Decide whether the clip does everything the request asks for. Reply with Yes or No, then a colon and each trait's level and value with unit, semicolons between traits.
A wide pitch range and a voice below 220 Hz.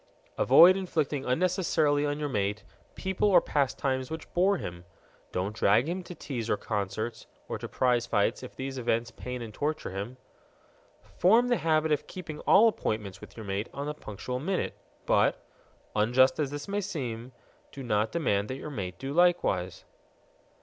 Yes: wide, 6.7 semitones; low, 135 Hz